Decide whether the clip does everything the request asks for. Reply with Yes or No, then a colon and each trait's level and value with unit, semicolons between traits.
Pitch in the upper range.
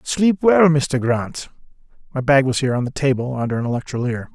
No: low, 135 Hz